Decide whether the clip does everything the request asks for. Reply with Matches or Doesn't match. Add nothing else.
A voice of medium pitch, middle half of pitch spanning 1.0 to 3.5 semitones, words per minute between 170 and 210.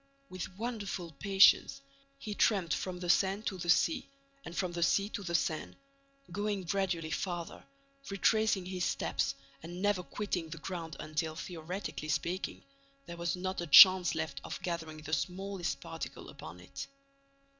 Doesn't match